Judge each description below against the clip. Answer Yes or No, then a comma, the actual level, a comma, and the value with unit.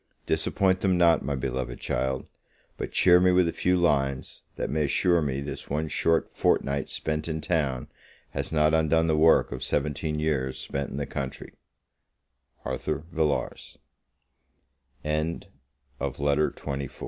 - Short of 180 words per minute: Yes, average, 155 wpm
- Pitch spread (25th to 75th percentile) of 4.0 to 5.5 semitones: No, average, 2.9 semitones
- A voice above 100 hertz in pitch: No, very low, 75 Hz